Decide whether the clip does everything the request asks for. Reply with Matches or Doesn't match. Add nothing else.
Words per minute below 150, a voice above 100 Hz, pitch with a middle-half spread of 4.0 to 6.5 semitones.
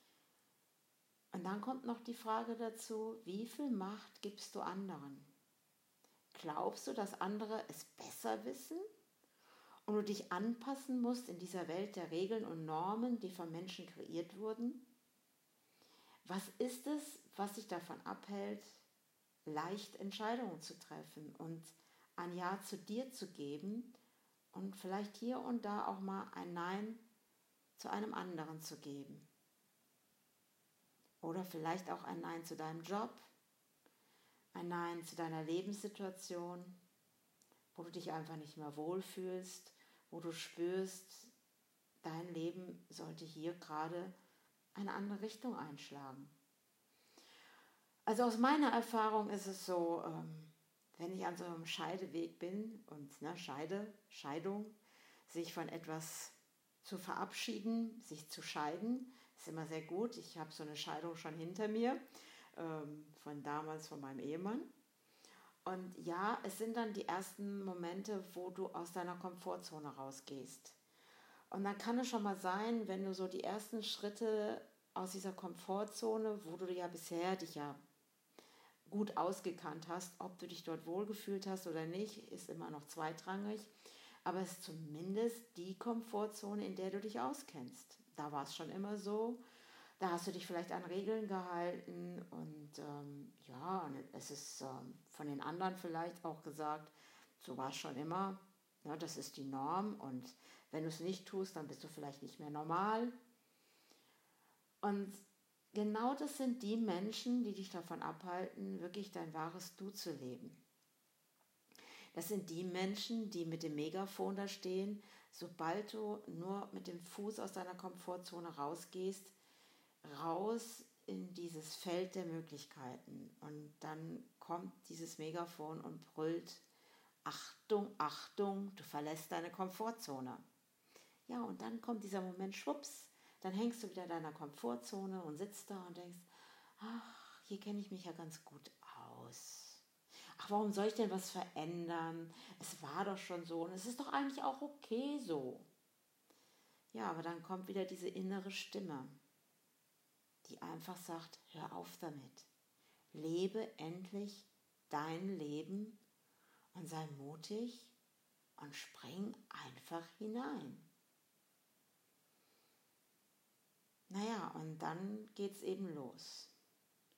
Matches